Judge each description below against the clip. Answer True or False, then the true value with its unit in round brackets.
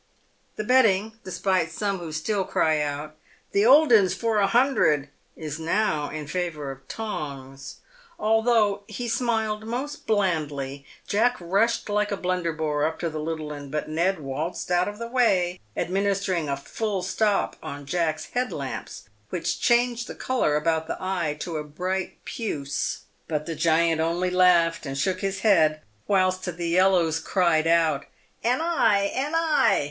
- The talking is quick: False (165 wpm)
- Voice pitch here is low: False (180 Hz)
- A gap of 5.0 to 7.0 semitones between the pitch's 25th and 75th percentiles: True (5.4 semitones)